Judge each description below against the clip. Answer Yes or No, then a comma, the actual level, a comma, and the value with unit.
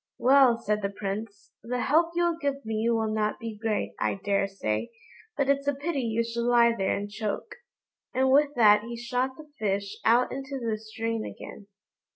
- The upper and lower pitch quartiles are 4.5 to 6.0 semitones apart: No, average, 4.0 semitones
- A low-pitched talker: No, high, 230 Hz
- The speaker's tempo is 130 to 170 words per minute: No, average, 185 wpm